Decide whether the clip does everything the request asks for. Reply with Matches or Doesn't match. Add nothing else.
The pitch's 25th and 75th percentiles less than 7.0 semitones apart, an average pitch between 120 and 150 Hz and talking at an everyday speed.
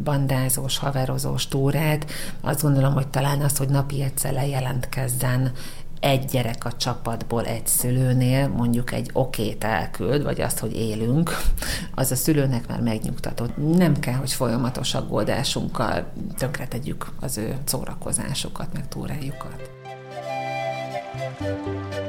Matches